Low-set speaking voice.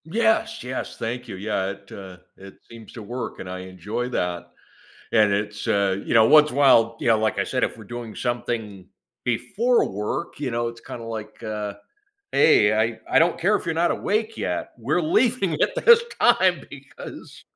Yes: low, 115 Hz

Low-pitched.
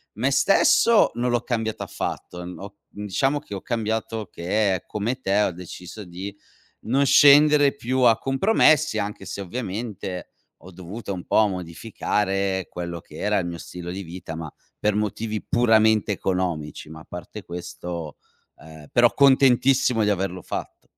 Yes: low, 105 Hz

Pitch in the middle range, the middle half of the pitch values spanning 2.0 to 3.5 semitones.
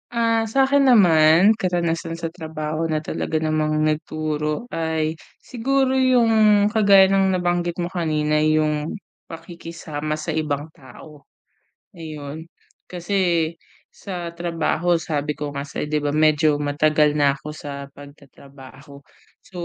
Yes: medium, 160 Hz; average, 2.8 semitones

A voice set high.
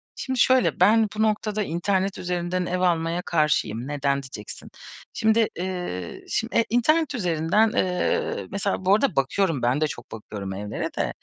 No: medium, 180 Hz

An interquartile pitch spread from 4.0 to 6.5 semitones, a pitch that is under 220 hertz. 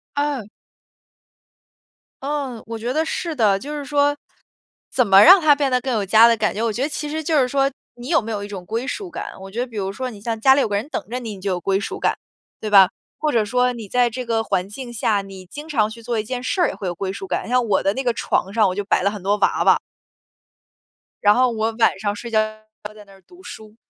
No: average, 4.4 semitones; high, 230 Hz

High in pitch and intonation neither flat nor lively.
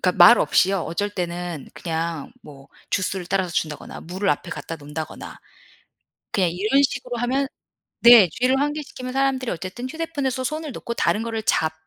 No: high, 205 Hz; wide, 6.9 semitones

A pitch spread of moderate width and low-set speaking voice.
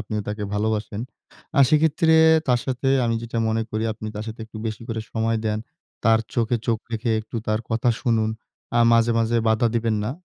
No: narrow, 1.4 semitones; low, 115 Hz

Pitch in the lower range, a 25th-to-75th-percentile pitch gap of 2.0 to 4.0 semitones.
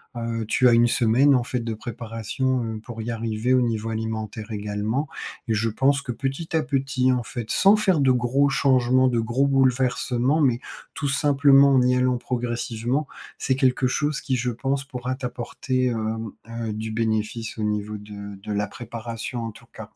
Yes: low, 120 Hz; average, 2.9 semitones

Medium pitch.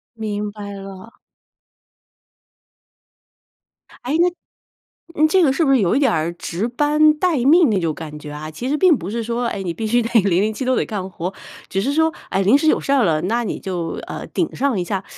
No: high, 225 Hz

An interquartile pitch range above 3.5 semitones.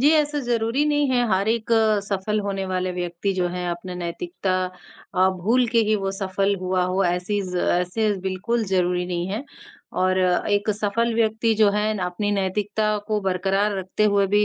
No: average, 2.9 semitones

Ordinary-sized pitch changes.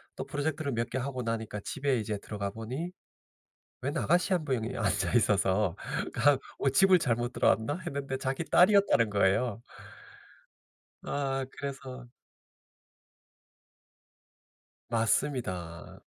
Yes: average, 4.5 semitones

